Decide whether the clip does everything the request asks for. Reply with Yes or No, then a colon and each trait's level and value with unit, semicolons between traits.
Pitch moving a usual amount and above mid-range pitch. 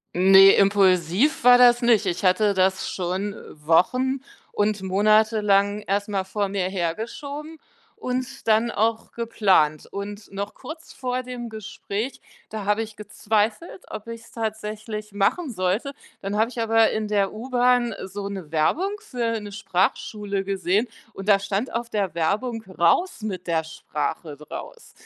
Yes: average, 3.1 semitones; high, 210 Hz